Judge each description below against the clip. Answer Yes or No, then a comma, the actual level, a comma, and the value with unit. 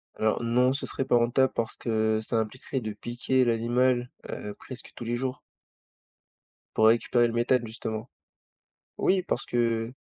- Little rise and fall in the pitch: Yes, narrow, 2.0 semitones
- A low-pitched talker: Yes, low, 120 Hz